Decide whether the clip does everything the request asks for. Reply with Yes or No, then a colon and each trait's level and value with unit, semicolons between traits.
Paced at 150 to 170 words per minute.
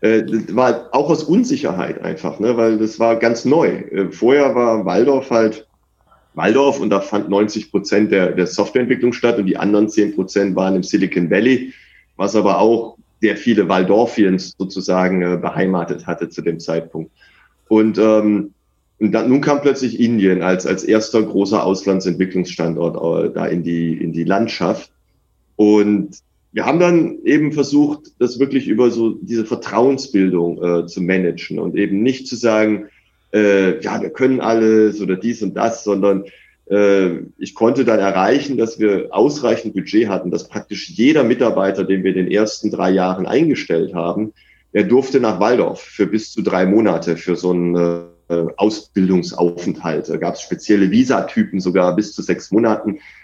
Yes: average, 160 wpm